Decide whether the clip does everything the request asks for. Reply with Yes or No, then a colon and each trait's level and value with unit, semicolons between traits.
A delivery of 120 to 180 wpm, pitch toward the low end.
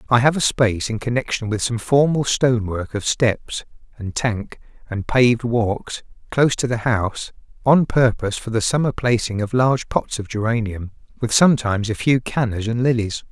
Yes: average, 175 wpm; low, 115 Hz